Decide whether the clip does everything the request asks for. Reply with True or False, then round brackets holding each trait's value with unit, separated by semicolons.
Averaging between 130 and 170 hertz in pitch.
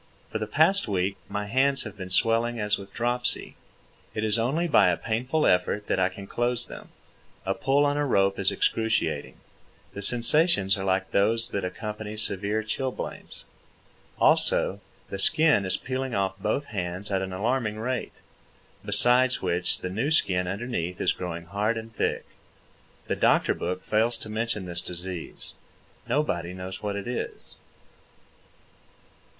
False (105 Hz)